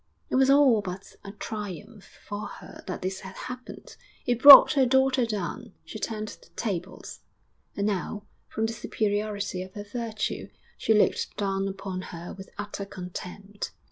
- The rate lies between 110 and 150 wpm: No, average, 160 wpm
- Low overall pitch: No, high, 205 Hz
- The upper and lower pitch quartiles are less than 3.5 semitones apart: Yes, average, 2.9 semitones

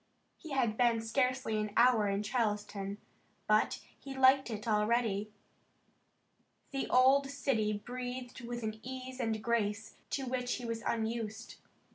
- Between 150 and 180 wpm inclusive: No, slow, 135 wpm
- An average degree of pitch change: Yes, average, 3.0 semitones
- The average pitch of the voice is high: Yes, high, 235 Hz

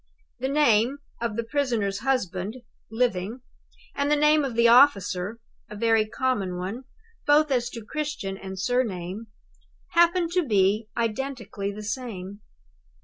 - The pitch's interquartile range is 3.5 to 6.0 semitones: Yes, average, 5.0 semitones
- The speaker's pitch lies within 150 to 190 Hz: No, high, 230 Hz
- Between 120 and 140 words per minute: Yes, slow, 135 wpm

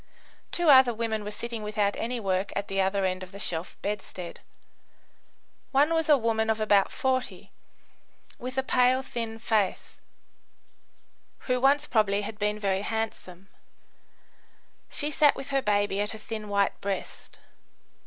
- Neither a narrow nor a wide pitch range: Yes, average, 3.9 semitones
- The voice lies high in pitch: Yes, high, 215 Hz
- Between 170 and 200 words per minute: No, average, 150 wpm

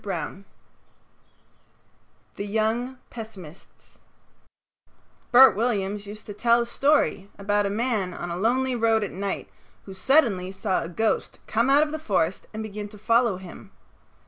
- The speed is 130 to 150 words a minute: Yes, average, 145 wpm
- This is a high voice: Yes, high, 210 Hz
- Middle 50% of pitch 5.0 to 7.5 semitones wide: No, average, 3.4 semitones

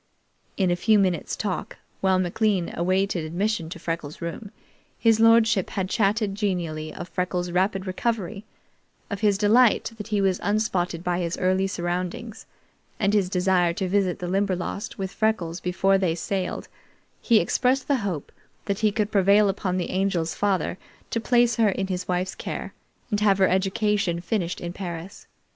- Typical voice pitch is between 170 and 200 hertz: Yes, high, 190 Hz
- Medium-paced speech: Yes, average, 165 wpm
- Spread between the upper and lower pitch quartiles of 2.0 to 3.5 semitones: Yes, average, 2.8 semitones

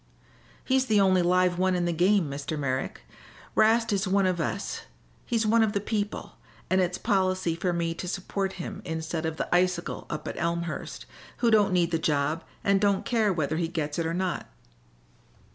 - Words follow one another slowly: No, average, 190 wpm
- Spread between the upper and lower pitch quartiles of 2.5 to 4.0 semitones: Yes, average, 3.2 semitones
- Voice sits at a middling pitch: Yes, medium, 180 Hz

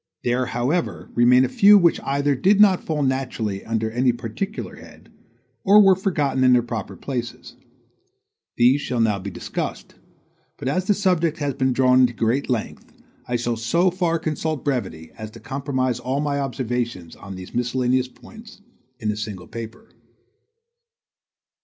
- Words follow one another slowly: No, average, 160 wpm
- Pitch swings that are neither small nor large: Yes, average, 4.6 semitones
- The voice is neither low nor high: No, low, 130 Hz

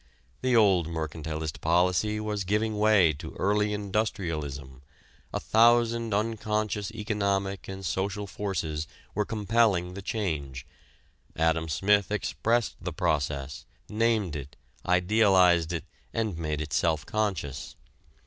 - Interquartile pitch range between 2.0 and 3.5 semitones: No, average, 5.0 semitones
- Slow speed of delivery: Yes, slow, 115 wpm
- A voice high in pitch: No, very low, 95 Hz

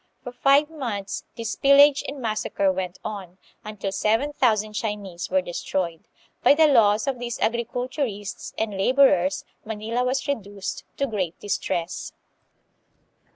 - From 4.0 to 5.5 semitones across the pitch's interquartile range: Yes, average, 4.7 semitones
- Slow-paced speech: Yes, slow, 130 wpm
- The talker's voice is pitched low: No, high, 215 Hz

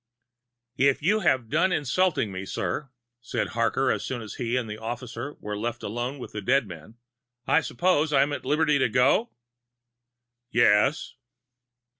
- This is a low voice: Yes, low, 125 Hz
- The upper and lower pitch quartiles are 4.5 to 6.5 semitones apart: Yes, average, 4.9 semitones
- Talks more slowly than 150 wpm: No, average, 160 wpm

